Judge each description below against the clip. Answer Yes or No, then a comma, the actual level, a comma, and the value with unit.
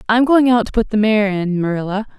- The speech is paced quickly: Yes, fast, 245 wpm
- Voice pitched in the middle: No, high, 215 Hz